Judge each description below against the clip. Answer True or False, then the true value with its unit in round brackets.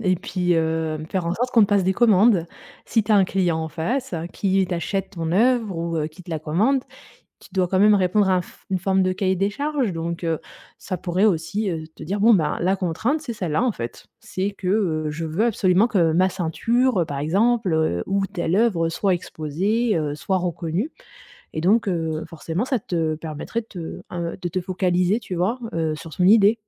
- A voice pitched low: False (185 Hz)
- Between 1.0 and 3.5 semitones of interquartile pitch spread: False (4.0 semitones)